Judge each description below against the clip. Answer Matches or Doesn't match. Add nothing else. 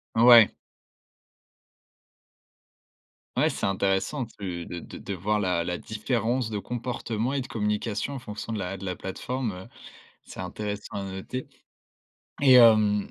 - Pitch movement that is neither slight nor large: Matches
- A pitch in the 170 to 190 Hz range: Doesn't match